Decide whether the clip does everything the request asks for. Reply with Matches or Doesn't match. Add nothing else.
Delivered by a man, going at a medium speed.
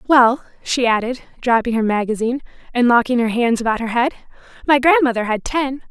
Doesn't match